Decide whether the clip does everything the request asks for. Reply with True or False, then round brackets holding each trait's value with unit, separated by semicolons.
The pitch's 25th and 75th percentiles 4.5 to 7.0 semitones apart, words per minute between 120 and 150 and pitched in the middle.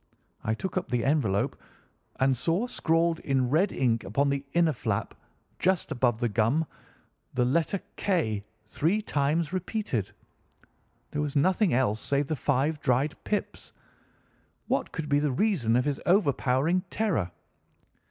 True (5.4 semitones; 145 wpm; 145 Hz)